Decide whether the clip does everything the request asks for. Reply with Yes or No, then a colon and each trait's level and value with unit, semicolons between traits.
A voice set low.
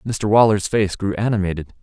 Yes: low, 100 Hz